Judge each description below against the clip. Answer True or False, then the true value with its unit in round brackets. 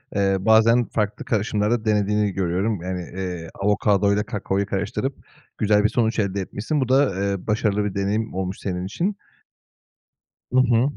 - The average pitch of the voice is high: False (105 Hz)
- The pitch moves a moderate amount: False (2.3 semitones)